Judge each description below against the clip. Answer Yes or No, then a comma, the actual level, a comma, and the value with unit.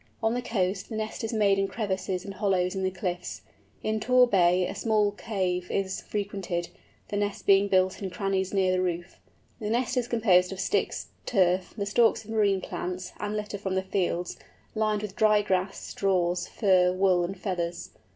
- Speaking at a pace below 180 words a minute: No, average, 190 wpm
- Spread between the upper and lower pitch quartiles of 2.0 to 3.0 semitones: Yes, narrow, 2.4 semitones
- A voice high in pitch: Yes, high, 195 Hz